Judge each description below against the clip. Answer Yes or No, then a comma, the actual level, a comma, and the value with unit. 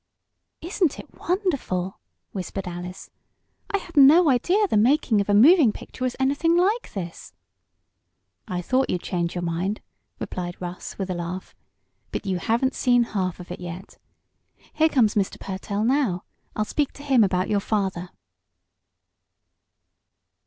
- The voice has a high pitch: Yes, high, 210 Hz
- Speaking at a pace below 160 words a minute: Yes, average, 145 wpm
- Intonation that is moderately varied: No, wide, 7.5 semitones